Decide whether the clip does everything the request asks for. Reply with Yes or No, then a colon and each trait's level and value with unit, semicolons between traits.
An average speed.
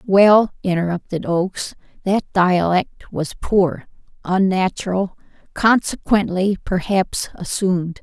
No: slow, 75 wpm